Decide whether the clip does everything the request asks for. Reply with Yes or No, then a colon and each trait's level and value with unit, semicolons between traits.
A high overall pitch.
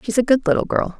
Yes: high, 230 Hz